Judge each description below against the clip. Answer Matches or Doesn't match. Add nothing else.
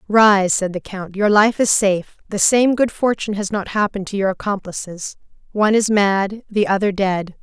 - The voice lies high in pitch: Matches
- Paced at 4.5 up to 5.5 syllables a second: Matches